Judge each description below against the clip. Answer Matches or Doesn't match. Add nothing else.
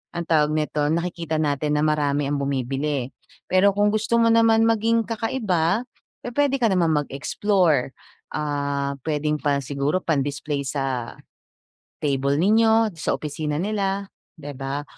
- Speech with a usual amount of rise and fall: Doesn't match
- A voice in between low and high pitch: Matches